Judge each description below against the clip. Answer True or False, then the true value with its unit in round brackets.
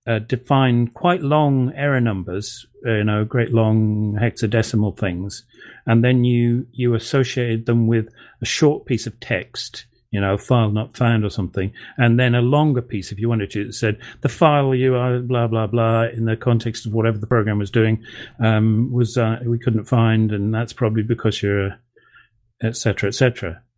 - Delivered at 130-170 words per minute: False (190 wpm)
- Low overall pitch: True (115 Hz)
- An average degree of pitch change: False (1.9 semitones)